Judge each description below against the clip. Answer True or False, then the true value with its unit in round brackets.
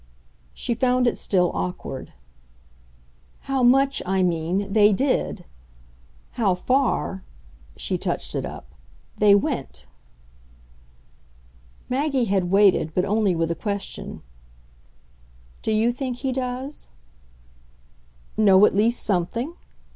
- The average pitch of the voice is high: True (210 Hz)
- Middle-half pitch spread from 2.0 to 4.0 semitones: False (5.1 semitones)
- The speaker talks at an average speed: False (110 wpm)